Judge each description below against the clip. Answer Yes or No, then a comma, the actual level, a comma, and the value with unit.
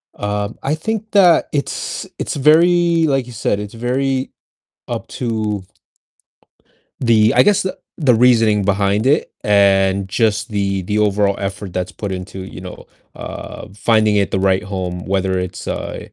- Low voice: Yes, low, 105 Hz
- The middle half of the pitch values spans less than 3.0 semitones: No, average, 4.9 semitones